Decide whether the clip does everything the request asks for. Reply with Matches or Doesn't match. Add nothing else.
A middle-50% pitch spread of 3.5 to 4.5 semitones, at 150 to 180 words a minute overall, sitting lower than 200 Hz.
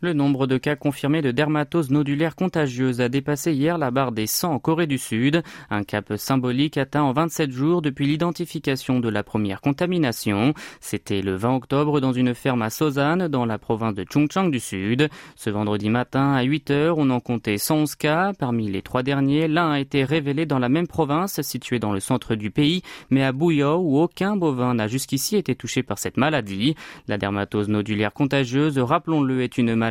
Doesn't match